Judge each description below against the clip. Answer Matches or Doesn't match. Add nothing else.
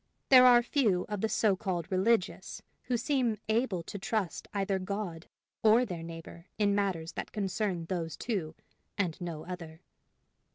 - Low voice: Doesn't match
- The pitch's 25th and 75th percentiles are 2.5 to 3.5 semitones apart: Doesn't match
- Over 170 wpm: Doesn't match